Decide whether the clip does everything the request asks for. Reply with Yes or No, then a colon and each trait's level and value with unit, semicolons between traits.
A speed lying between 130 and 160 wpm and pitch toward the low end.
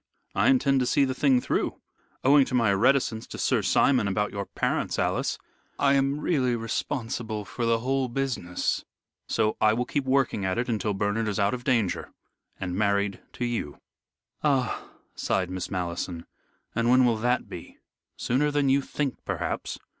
No: average, 170 wpm; low, 120 Hz